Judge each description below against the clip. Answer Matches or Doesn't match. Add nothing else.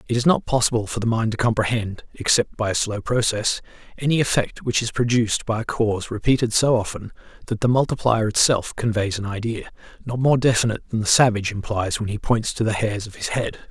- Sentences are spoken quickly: Matches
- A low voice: Matches